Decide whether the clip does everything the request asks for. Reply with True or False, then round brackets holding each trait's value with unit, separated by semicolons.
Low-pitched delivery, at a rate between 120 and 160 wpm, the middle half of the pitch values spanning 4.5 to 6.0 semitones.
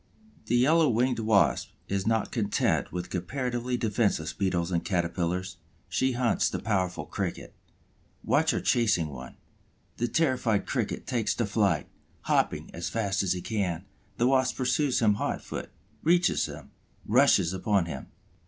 True (105 Hz; 145 wpm; 5.2 semitones)